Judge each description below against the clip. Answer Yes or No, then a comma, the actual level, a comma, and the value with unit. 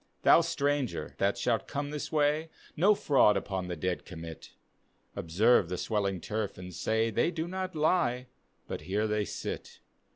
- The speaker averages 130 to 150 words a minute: No, average, 165 wpm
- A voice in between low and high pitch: No, low, 115 Hz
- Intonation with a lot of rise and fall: Yes, wide, 7.4 semitones